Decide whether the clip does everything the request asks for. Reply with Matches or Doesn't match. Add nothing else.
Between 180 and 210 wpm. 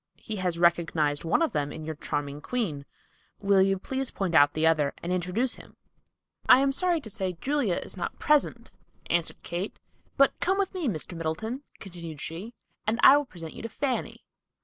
Matches